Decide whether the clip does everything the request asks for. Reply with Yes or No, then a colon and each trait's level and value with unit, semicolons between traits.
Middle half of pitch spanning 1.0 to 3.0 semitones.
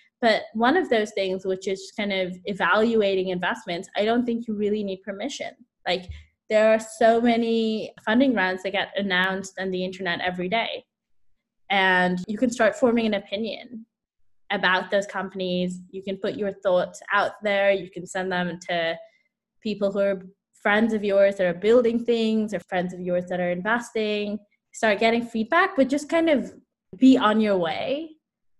No: average, 3.5 semitones